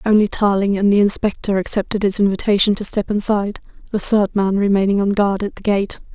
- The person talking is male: No, female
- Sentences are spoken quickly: No, average, 195 wpm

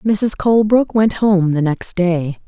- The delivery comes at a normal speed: Yes, average, 170 wpm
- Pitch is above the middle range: Yes, high, 195 Hz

